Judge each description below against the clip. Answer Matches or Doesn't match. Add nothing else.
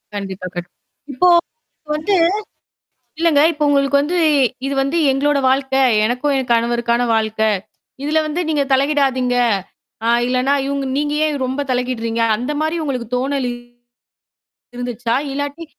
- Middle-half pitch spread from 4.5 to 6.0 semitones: Doesn't match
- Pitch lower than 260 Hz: Doesn't match